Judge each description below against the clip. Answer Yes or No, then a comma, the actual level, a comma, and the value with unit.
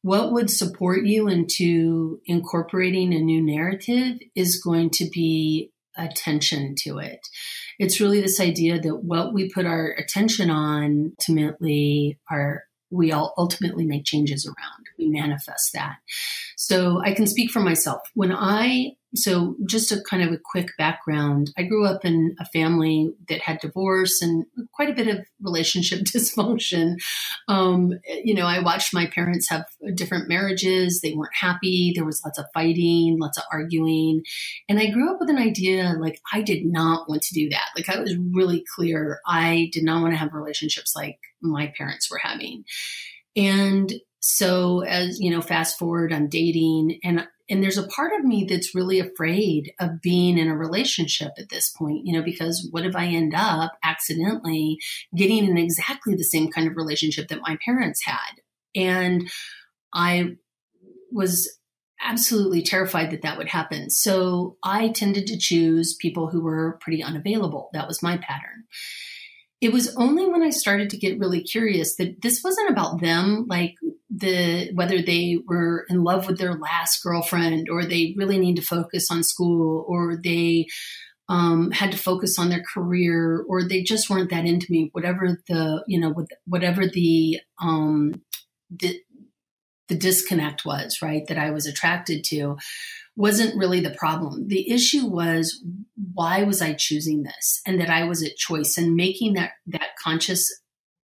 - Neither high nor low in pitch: Yes, medium, 175 Hz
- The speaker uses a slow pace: No, average, 170 wpm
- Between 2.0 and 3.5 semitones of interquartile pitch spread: Yes, average, 3.0 semitones